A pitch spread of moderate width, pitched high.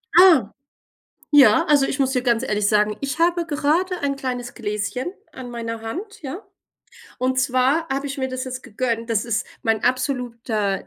Yes: average, 3.7 semitones; very high, 255 Hz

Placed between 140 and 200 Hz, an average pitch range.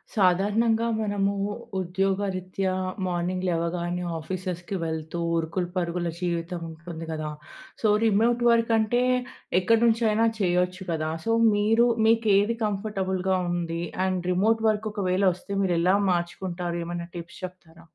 Yes: medium, 185 Hz; average, 3.2 semitones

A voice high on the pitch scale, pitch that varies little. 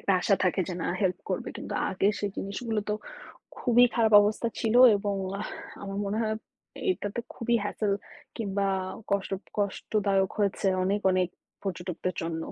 Yes: high, 200 Hz; narrow, 2.0 semitones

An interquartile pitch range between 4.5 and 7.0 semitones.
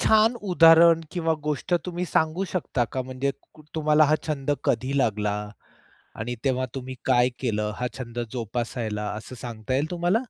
Yes: average, 5.1 semitones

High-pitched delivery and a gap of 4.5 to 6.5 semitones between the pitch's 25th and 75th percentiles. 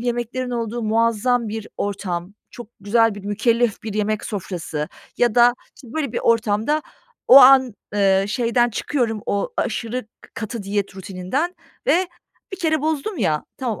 No: high, 230 Hz; average, 3.4 semitones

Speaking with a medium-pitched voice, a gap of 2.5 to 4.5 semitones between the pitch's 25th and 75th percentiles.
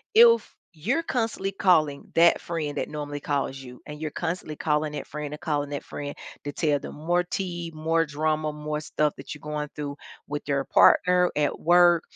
Yes: medium, 150 Hz; average, 2.8 semitones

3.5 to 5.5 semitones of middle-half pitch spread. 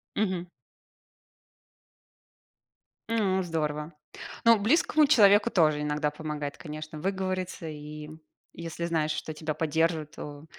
Yes: average, 3.8 semitones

